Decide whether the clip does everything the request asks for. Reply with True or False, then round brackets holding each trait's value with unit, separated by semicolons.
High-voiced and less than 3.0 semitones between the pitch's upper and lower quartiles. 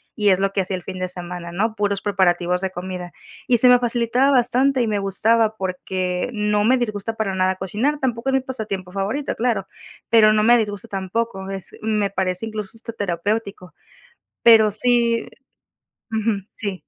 False (210 Hz; 3.5 semitones)